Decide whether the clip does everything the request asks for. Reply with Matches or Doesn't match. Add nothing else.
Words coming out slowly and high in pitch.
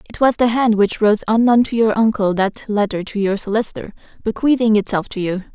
Doesn't match